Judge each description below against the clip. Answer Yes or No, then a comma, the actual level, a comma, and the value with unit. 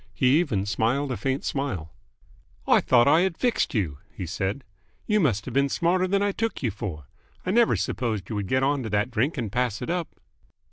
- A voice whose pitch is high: No, low, 130 Hz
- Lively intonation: Yes, wide, 7.9 semitones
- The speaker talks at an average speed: No, fast, 215 wpm